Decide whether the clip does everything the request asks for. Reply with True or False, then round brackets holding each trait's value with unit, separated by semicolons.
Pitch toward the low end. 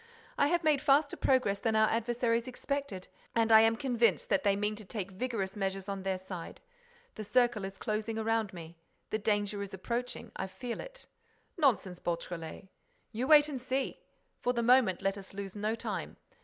False (220 Hz)